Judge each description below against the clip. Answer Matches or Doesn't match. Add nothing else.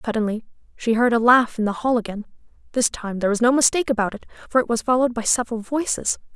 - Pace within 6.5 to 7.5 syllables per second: Matches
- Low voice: Doesn't match